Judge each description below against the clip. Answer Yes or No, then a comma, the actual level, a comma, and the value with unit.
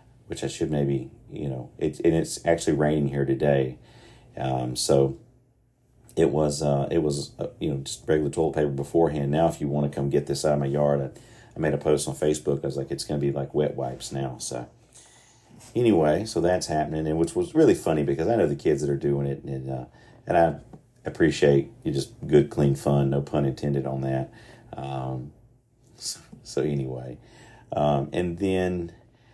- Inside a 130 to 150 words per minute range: No, average, 200 wpm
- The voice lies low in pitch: Yes, very low, 75 Hz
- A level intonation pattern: No, average, 3.5 semitones